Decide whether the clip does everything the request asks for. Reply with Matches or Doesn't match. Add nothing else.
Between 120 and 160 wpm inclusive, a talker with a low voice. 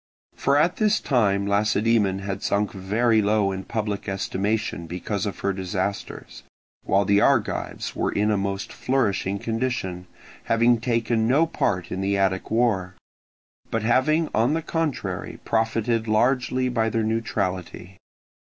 Matches